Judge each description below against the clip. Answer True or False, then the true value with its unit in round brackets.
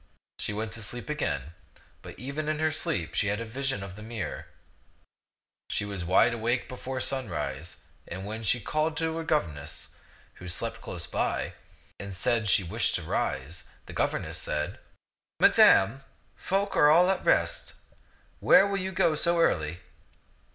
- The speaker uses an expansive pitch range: True (8.0 semitones)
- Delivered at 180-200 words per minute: False (155 wpm)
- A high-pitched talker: False (115 Hz)